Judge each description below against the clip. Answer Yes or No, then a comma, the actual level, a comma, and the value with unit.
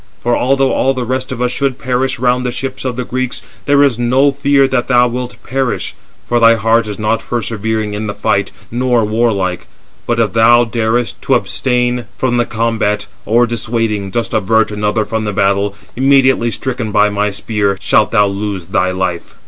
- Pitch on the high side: No, low, 115 Hz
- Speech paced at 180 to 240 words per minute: Yes, average, 190 wpm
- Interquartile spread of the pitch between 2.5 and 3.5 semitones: Yes, average, 3.1 semitones